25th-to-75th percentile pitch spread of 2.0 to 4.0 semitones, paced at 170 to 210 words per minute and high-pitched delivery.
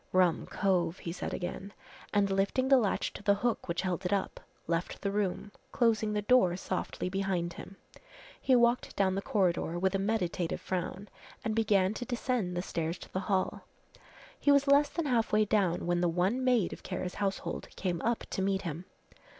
Yes: average, 3.5 semitones; average, 190 wpm; high, 195 Hz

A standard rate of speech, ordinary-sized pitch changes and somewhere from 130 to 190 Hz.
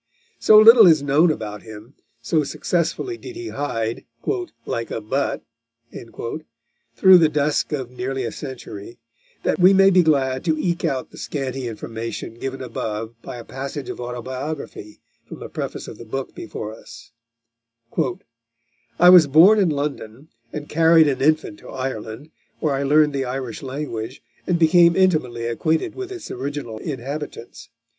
Yes: average, 155 wpm; average, 5.0 semitones; medium, 140 Hz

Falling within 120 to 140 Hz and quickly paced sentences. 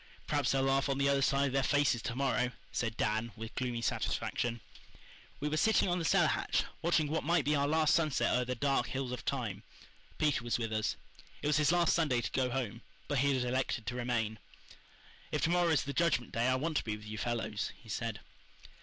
Yes: low, 135 Hz; fast, 225 wpm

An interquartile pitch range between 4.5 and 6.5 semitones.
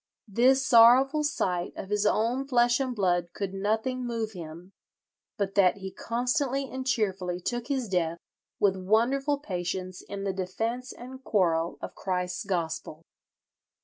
Yes: wide, 5.4 semitones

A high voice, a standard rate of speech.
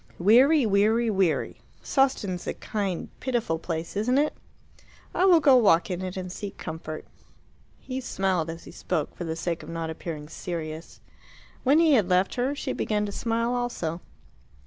Yes: high, 195 Hz; average, 170 wpm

